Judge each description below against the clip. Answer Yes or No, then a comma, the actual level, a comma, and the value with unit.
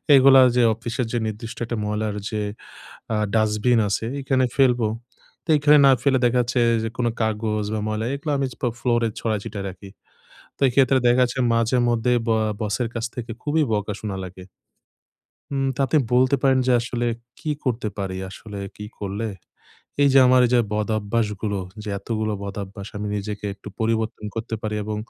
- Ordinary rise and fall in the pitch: Yes, average, 3.0 semitones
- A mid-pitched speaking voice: No, low, 115 Hz